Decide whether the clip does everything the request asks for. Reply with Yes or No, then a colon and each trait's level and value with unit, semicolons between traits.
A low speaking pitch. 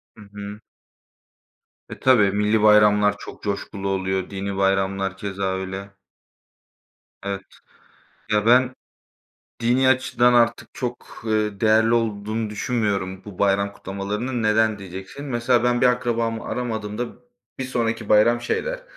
Yes: low, 105 Hz